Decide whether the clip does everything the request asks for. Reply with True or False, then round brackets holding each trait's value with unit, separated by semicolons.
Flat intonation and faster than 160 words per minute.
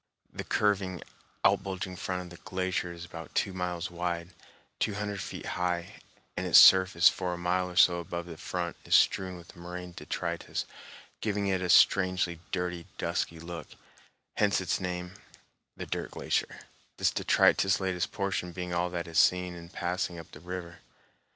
True (1.2 semitones; 170 wpm)